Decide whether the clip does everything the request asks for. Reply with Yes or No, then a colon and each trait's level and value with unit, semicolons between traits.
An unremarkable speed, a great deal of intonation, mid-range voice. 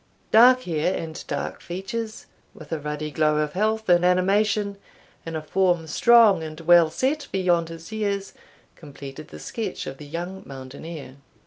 No: average, 155 wpm; average, 4.8 semitones; medium, 175 Hz